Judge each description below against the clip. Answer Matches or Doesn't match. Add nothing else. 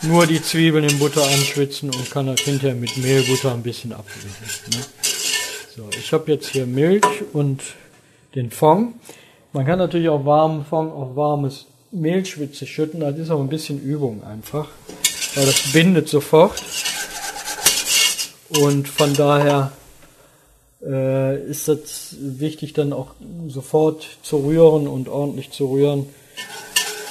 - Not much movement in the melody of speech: Matches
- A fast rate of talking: Doesn't match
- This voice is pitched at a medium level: Matches